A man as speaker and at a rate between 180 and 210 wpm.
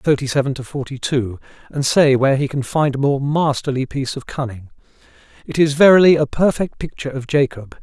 Yes: male; average, 190 wpm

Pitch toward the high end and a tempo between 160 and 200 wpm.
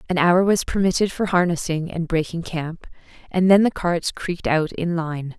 No: medium, 175 Hz; average, 190 wpm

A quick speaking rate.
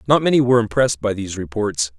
Yes: fast, 210 wpm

